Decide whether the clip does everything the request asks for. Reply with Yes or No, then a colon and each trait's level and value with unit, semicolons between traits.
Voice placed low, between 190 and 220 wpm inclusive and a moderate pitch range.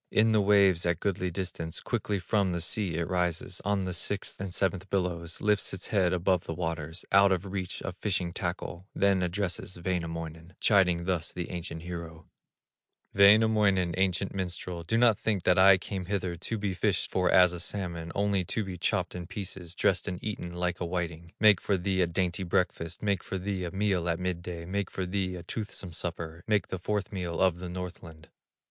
No: very low, 90 Hz; average, 195 wpm; narrow, 2.2 semitones